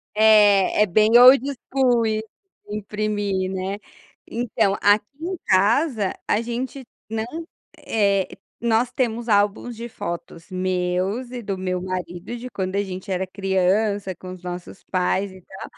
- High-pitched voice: Yes, high, 205 Hz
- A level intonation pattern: No, average, 3.4 semitones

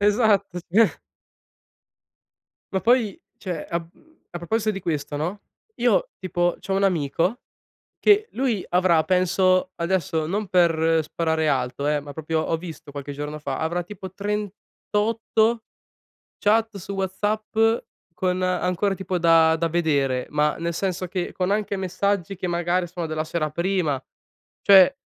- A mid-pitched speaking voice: Yes, medium, 180 Hz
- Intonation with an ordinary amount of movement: Yes, average, 3.7 semitones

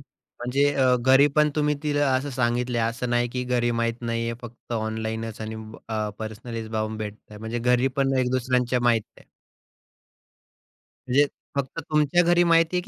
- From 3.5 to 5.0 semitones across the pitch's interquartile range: No, average, 2.9 semitones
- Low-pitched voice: Yes, low, 120 Hz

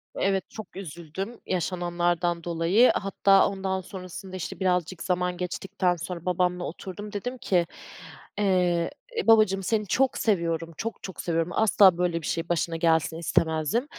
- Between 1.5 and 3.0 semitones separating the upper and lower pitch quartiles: Yes, narrow, 2.4 semitones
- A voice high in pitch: No, medium, 180 Hz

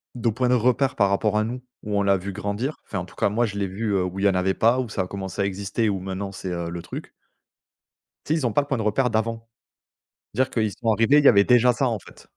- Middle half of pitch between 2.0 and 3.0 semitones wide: No, average, 3.7 semitones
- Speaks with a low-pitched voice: Yes, low, 105 Hz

